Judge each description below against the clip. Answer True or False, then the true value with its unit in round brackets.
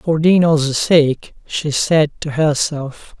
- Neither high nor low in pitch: True (150 Hz)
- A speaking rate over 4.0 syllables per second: False (3.1 syllables/s)